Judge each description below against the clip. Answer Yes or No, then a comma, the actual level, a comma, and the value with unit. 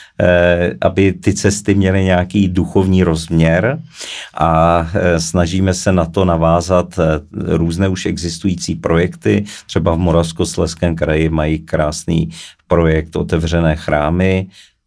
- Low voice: Yes, very low, 90 Hz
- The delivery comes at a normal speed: No, slow, 105 wpm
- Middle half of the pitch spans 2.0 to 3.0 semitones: Yes, narrow, 2.5 semitones